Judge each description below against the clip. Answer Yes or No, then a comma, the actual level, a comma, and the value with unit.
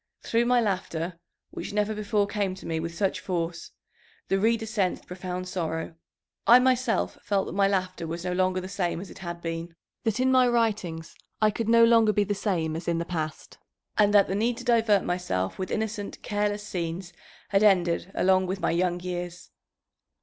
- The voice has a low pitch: No, high, 190 Hz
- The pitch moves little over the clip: No, average, 3.5 semitones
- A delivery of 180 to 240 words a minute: Yes, average, 195 wpm